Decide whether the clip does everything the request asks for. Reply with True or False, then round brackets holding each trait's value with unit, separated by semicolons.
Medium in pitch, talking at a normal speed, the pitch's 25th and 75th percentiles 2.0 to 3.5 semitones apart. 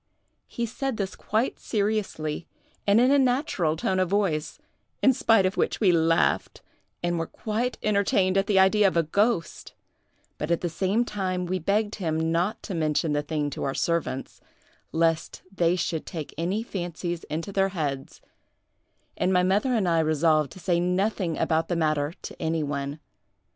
False (180 Hz; 175 wpm; 4.0 semitones)